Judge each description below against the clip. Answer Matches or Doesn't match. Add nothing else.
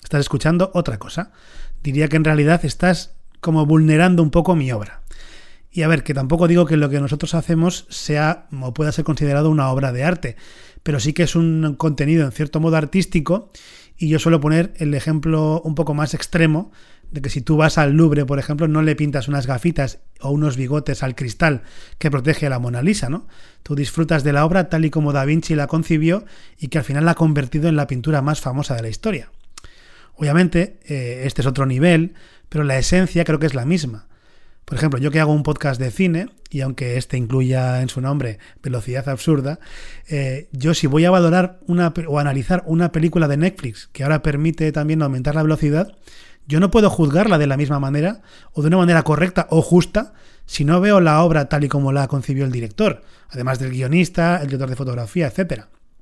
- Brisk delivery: Matches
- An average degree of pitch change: Matches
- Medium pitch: Matches